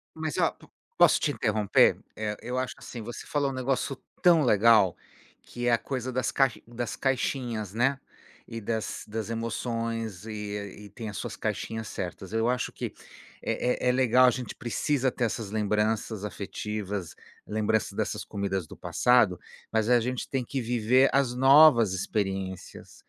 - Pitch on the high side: No, low, 115 Hz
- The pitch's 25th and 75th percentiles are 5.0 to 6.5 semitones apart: No, average, 3.2 semitones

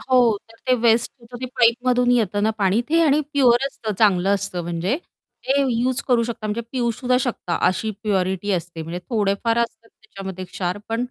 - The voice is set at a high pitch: Yes, high, 225 Hz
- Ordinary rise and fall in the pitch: Yes, average, 3.9 semitones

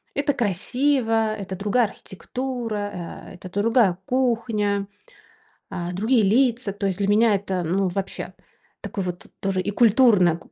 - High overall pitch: Yes, high, 205 Hz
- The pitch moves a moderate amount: Yes, average, 3.7 semitones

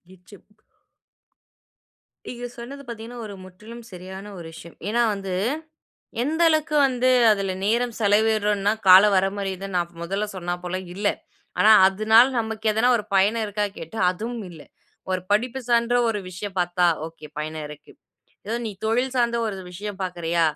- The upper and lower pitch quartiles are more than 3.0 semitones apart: Yes, average, 3.9 semitones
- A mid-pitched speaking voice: No, high, 205 Hz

